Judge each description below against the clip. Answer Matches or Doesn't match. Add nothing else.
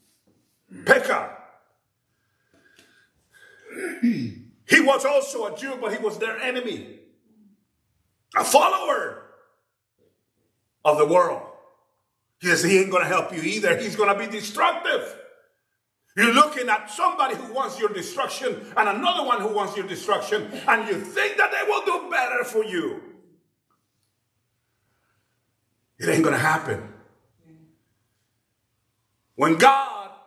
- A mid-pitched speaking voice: Doesn't match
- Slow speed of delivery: Matches